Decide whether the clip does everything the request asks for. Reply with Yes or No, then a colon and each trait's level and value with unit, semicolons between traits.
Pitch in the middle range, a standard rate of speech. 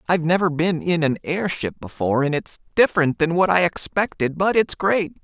Yes: medium, 165 Hz; average, 195 wpm